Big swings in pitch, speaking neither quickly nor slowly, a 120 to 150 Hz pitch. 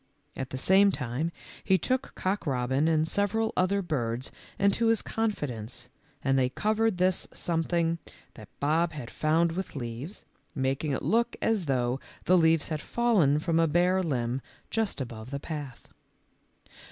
No: wide, 6.0 semitones; average, 155 wpm; medium, 160 Hz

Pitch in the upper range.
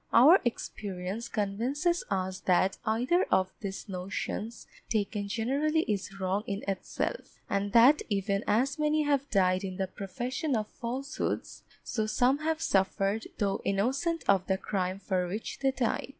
Yes: high, 215 Hz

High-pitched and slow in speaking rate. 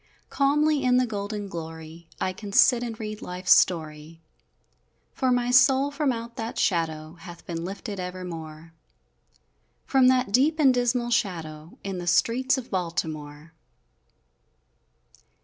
Yes: high, 200 Hz; slow, 130 wpm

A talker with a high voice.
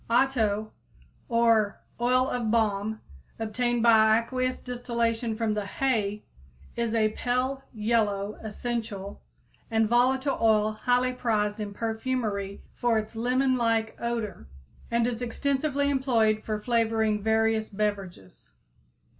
Yes: high, 225 Hz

